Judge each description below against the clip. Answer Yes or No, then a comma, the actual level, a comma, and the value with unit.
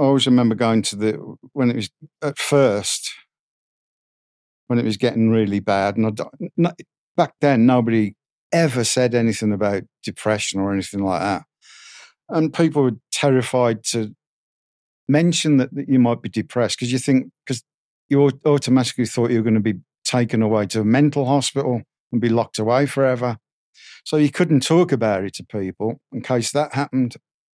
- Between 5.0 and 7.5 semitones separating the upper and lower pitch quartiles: No, average, 4.0 semitones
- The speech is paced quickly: No, average, 170 wpm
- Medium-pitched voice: No, low, 120 Hz